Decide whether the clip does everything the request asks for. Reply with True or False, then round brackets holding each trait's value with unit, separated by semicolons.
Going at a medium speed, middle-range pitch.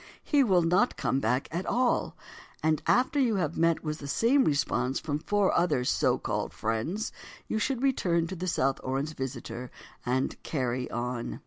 True (175 wpm; 155 Hz)